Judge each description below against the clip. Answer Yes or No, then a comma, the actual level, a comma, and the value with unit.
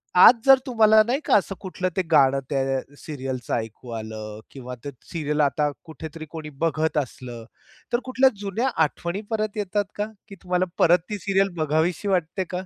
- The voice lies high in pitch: No, medium, 165 Hz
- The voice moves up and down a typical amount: No, wide, 6.4 semitones